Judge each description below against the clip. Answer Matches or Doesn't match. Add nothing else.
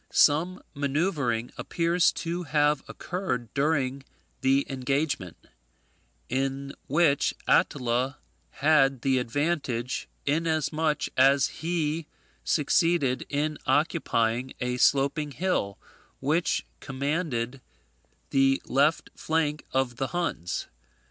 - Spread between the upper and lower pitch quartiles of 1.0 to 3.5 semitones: Matches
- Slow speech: Matches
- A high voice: Doesn't match